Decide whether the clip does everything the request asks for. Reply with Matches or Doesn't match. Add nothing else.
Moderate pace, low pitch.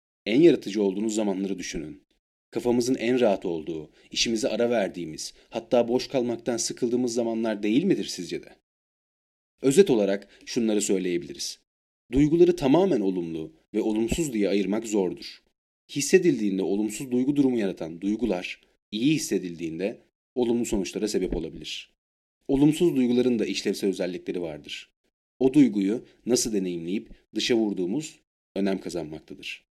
Matches